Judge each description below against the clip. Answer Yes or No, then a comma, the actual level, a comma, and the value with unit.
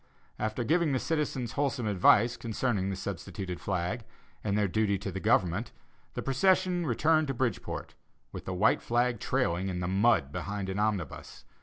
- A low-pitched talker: Yes, low, 110 Hz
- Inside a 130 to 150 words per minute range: No, average, 165 wpm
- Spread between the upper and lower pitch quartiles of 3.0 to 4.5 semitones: No, average, 5.2 semitones